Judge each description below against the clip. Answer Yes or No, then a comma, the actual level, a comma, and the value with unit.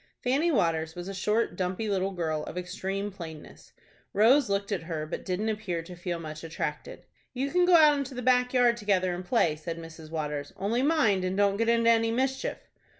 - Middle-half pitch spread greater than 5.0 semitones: Yes, wide, 5.6 semitones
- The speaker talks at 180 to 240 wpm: Yes, fast, 205 wpm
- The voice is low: No, high, 195 Hz